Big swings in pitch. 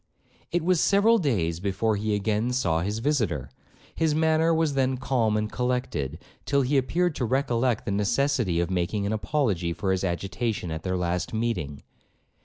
Yes: wide, 7.0 semitones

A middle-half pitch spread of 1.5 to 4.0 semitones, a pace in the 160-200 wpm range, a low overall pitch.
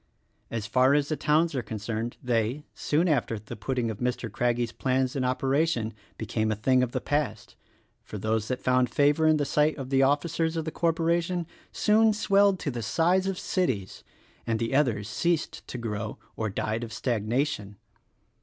No: wide, 5.6 semitones; average, 185 wpm; low, 130 Hz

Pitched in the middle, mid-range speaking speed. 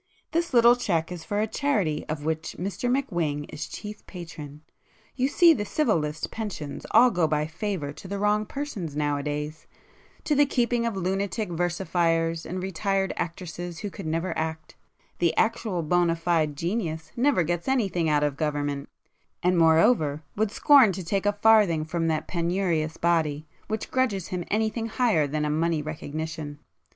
Yes: medium, 175 Hz; average, 160 wpm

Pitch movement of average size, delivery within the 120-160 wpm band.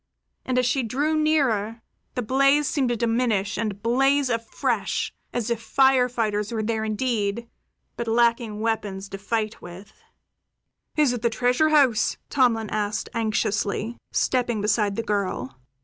Yes: average, 3.0 semitones; average, 145 wpm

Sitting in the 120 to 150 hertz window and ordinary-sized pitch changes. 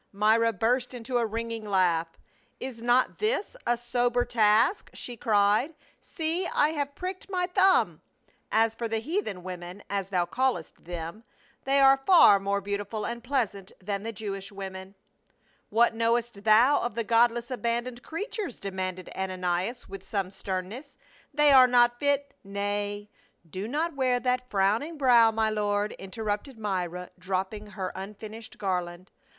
No: high, 225 Hz; average, 4.1 semitones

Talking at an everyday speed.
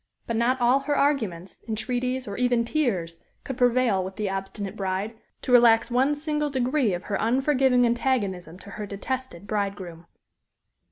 Yes: average, 155 wpm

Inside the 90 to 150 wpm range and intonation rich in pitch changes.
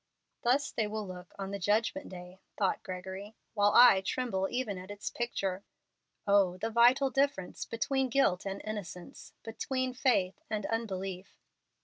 No: average, 145 wpm; average, 4.0 semitones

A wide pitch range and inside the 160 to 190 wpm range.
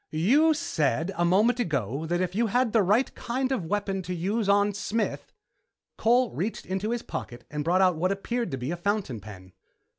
No: wide, 5.7 semitones; fast, 205 wpm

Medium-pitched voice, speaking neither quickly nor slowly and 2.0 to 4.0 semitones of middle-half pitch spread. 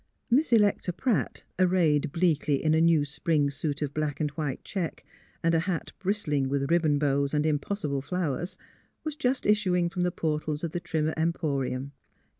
Yes: medium, 160 Hz; average, 175 wpm; average, 3.6 semitones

